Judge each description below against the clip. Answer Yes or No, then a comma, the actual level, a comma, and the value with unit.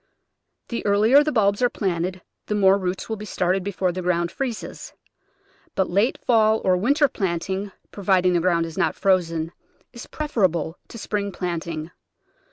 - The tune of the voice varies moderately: Yes, average, 3.3 semitones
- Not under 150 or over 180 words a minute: Yes, average, 165 wpm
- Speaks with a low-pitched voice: No, high, 190 Hz